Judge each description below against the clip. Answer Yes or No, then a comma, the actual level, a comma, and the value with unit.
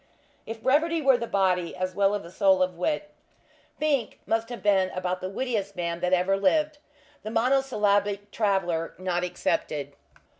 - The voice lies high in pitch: Yes, high, 200 Hz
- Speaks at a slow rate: No, average, 160 wpm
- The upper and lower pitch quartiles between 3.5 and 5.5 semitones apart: Yes, average, 4.4 semitones